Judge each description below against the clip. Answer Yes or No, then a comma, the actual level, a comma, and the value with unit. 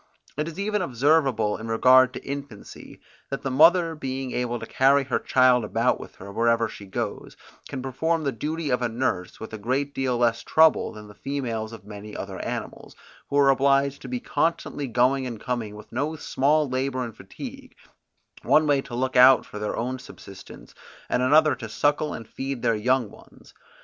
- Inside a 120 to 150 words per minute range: No, average, 190 wpm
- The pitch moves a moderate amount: Yes, average, 3.5 semitones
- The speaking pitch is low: Yes, low, 130 Hz